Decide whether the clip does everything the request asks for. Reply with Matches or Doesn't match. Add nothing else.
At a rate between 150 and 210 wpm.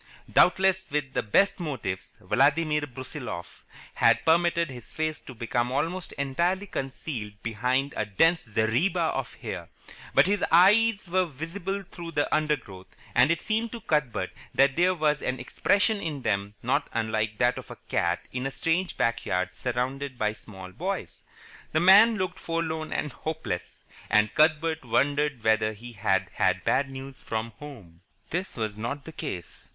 Matches